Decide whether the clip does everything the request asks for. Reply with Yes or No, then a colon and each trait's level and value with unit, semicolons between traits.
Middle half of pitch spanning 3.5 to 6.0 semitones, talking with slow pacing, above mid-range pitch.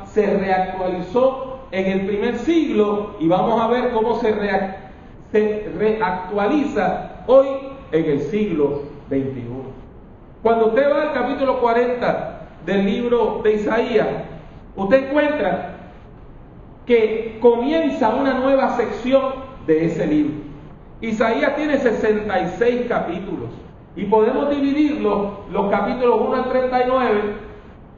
Yes: average, 4.9 semitones; slow, 105 wpm; high, 225 Hz